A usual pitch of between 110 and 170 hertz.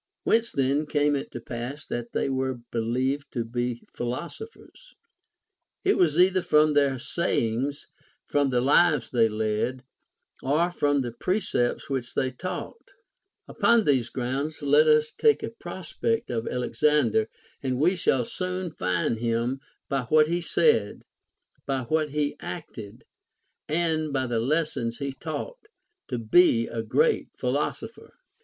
Yes: medium, 140 Hz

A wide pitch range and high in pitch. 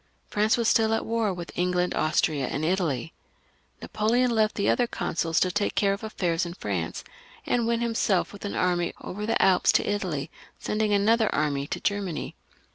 No: average, 4.5 semitones; high, 195 Hz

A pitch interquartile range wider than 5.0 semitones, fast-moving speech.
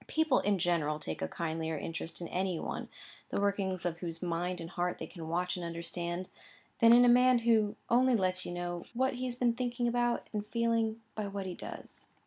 Yes: wide, 5.4 semitones; fast, 210 wpm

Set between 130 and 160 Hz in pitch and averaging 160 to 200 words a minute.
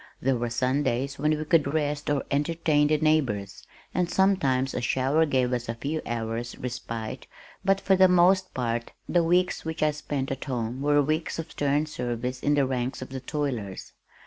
Yes: medium, 140 Hz; average, 185 wpm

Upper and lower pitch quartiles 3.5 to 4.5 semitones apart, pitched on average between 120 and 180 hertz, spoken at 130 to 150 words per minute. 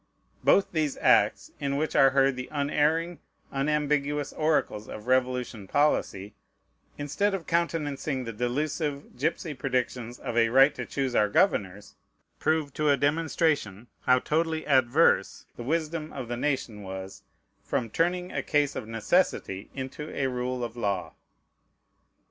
Yes: average, 4.1 semitones; medium, 140 Hz; average, 140 wpm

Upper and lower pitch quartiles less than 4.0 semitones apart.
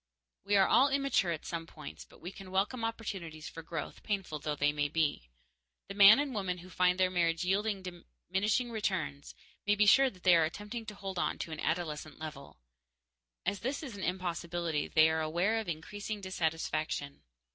No: average, 4.3 semitones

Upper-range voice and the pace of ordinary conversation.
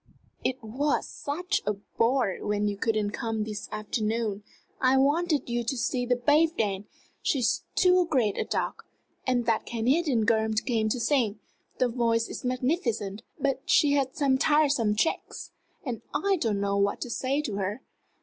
Yes: high, 240 Hz; average, 160 wpm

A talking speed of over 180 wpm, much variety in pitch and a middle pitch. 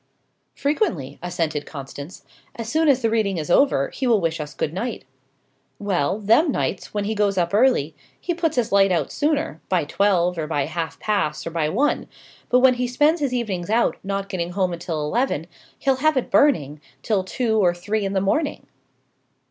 No: average, 190 wpm; wide, 6.7 semitones; high, 200 Hz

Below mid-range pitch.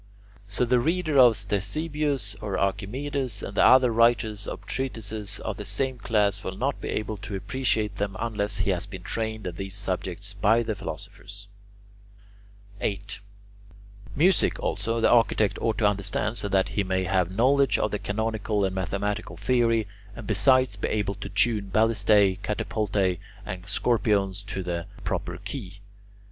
Yes: low, 105 Hz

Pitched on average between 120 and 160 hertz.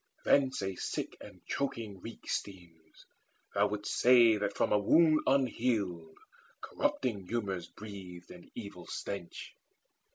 No: low, 100 Hz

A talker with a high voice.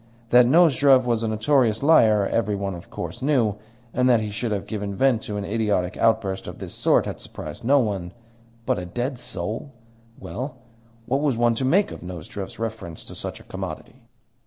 No: low, 115 Hz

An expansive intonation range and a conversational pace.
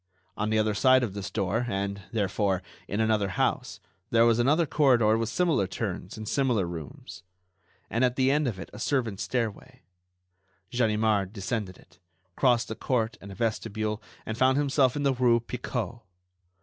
No: average, 3.7 semitones; average, 170 wpm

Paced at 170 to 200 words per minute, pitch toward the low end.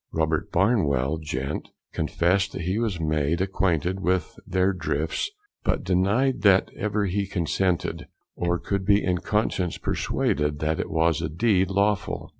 No: average, 145 wpm; very low, 90 Hz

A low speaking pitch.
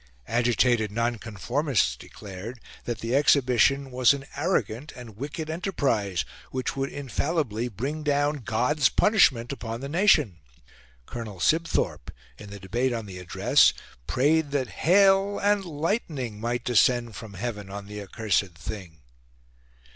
Yes: low, 120 Hz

